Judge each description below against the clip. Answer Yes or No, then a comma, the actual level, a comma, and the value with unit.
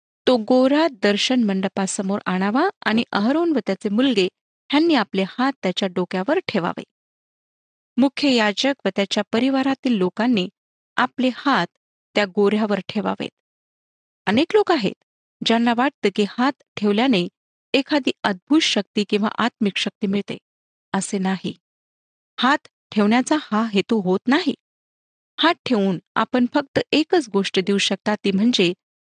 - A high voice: Yes, high, 220 Hz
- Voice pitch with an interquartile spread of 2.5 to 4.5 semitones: No, average, 5.0 semitones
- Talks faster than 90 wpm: Yes, average, 125 wpm